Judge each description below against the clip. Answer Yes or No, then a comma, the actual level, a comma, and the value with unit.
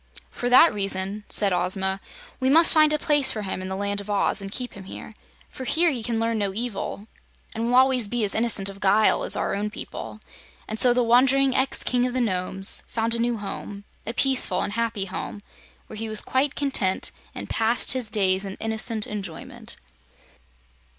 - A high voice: Yes, high, 220 Hz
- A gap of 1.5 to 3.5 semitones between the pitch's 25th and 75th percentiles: No, average, 3.9 semitones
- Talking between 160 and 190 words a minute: No, average, 200 wpm